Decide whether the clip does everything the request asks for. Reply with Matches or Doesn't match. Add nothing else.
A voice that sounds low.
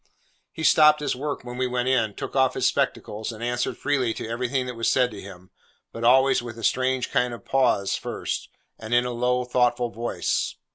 Matches